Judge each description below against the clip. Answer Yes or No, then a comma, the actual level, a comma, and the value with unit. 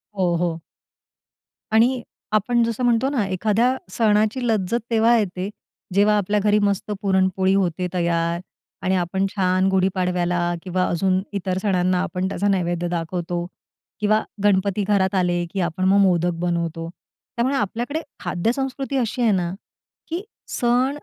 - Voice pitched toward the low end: No, high, 190 Hz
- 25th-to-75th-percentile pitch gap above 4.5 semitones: No, average, 3.5 semitones